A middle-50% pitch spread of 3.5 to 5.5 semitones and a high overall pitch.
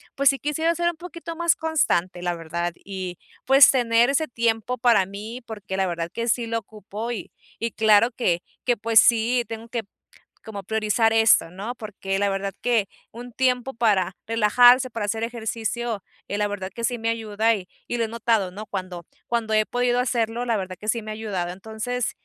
No: average, 3.1 semitones; high, 225 Hz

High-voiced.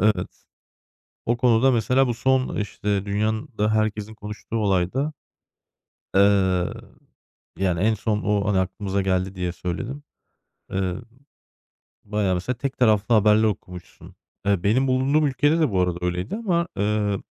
No: low, 105 Hz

